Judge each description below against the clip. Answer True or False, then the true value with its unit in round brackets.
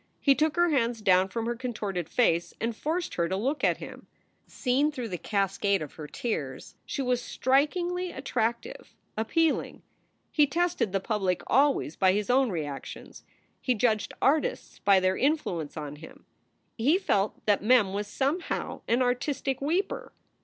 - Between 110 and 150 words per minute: False (165 wpm)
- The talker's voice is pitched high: True (235 Hz)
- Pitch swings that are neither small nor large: False (6.4 semitones)